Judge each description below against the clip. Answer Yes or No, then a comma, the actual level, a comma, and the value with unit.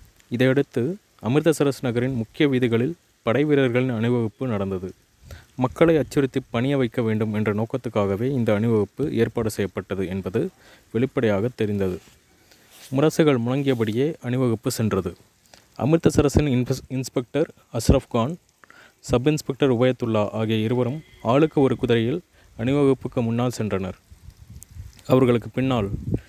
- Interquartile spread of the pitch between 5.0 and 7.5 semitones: No, average, 3.8 semitones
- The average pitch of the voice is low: Yes, low, 120 Hz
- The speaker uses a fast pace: No, average, 100 wpm